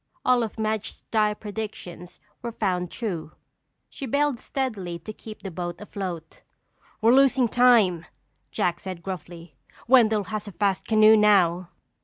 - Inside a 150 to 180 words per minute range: No, average, 140 wpm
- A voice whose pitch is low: No, high, 210 Hz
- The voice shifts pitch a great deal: No, average, 4.0 semitones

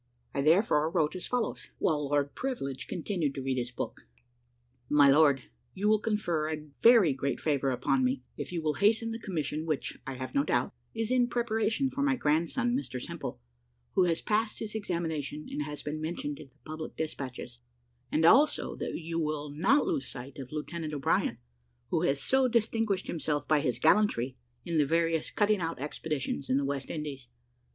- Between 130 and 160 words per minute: No, average, 185 wpm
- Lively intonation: Yes, wide, 6.8 semitones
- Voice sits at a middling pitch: Yes, medium, 155 Hz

